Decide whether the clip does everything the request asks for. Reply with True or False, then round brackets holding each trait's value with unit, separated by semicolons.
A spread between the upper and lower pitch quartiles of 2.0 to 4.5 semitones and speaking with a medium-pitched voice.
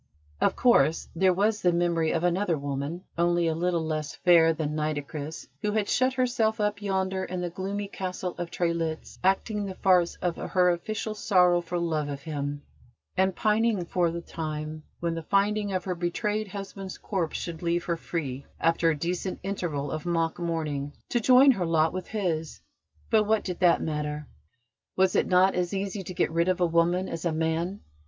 True (3.1 semitones; 175 Hz)